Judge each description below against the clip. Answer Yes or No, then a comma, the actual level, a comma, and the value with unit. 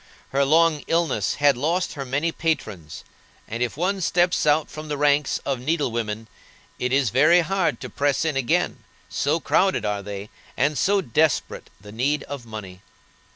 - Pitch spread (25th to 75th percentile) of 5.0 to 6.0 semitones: Yes, wide, 5.4 semitones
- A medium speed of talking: Yes, average, 170 wpm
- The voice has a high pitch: No, medium, 145 Hz